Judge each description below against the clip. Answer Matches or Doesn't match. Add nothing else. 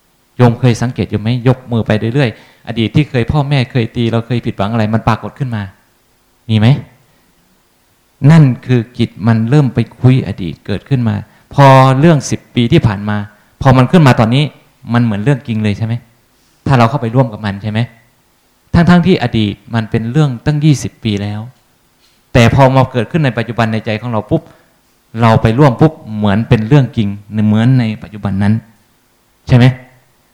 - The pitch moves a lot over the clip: Doesn't match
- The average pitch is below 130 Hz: Matches